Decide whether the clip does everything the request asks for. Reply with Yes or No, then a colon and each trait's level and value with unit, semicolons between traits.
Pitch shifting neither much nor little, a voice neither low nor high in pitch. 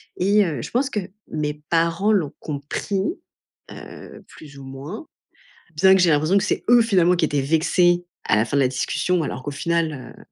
Yes: average, 4.7 semitones; medium, 165 Hz